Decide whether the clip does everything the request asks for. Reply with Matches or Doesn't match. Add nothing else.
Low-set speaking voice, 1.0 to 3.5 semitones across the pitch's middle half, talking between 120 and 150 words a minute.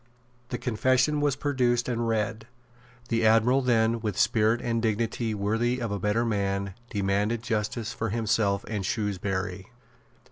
Matches